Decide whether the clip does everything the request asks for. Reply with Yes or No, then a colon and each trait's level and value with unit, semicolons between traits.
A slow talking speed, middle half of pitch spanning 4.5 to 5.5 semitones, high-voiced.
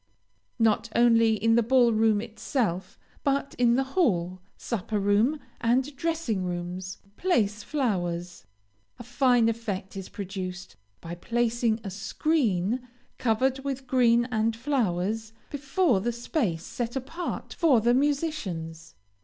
Yes: slow, 125 wpm; average, 5.1 semitones; high, 230 Hz